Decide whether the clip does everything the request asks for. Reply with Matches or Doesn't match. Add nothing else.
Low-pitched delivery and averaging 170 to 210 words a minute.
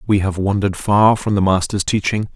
Matches